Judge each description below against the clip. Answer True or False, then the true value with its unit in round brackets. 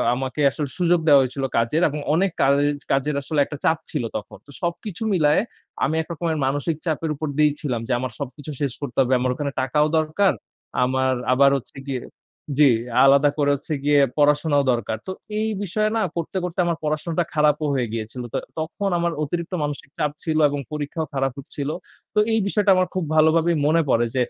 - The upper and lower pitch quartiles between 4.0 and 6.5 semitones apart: False (3.3 semitones)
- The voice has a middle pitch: True (150 Hz)